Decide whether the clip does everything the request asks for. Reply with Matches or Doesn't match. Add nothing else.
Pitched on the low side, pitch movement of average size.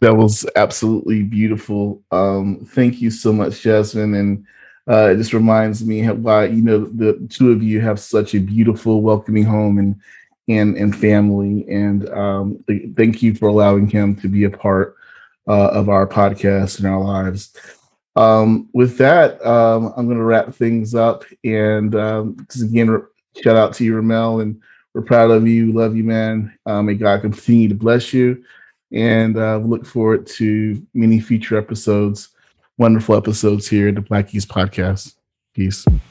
Doesn't match